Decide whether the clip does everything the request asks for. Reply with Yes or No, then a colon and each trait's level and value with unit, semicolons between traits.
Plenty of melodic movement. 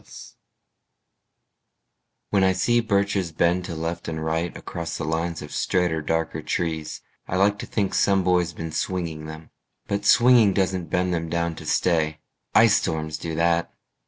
No: average, 2.7 semitones